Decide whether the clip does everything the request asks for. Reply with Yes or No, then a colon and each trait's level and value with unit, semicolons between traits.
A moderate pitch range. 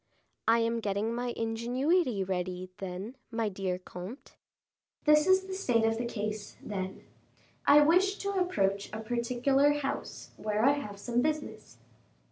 No: wide, 6.0 semitones